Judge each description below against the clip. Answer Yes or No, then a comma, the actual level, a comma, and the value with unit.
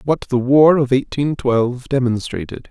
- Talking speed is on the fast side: No, average, 155 wpm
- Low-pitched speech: Yes, low, 130 Hz